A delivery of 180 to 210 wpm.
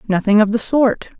Yes: average, 200 wpm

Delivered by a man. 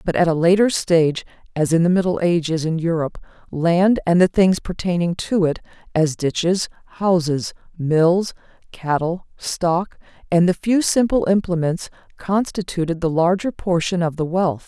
No: female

